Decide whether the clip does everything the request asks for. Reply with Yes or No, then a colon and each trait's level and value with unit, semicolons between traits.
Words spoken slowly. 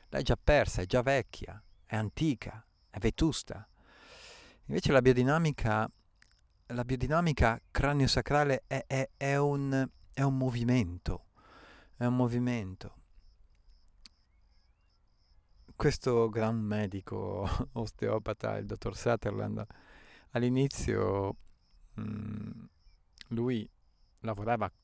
Yes: slow, 90 wpm